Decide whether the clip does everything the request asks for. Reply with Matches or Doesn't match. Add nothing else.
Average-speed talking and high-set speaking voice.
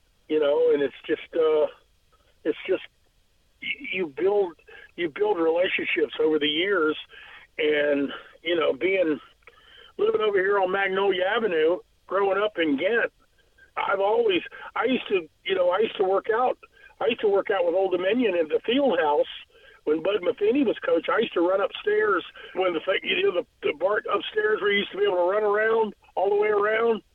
Matches